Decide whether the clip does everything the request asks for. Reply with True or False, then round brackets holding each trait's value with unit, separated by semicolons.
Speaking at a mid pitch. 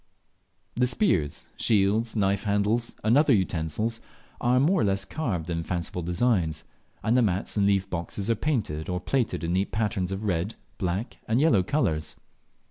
False (100 Hz)